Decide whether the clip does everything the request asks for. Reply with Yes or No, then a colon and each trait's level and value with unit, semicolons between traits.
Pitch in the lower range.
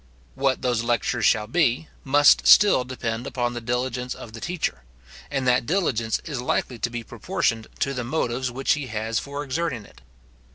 Yes: low, 125 Hz